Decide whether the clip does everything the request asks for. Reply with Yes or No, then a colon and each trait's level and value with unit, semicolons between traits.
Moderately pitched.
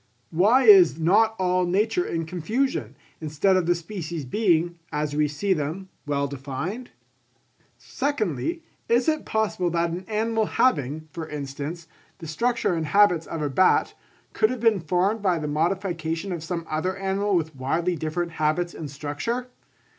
Yes: medium, 175 Hz